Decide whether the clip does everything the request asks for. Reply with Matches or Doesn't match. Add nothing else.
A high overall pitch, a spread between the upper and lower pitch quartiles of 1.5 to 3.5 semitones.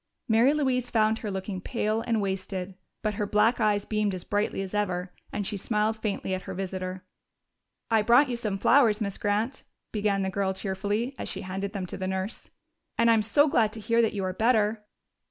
Matches